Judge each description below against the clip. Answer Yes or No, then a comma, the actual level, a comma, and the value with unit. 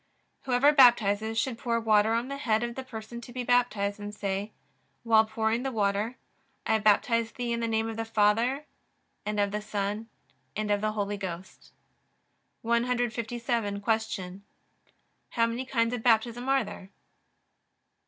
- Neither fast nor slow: Yes, average, 155 wpm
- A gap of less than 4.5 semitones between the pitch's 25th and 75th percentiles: Yes, narrow, 2.4 semitones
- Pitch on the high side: Yes, high, 225 Hz